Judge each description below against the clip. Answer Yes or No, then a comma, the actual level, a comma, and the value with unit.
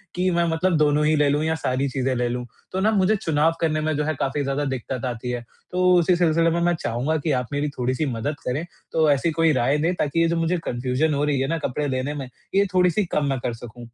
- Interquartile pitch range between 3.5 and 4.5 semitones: Yes, average, 4.1 semitones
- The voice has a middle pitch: Yes, medium, 150 Hz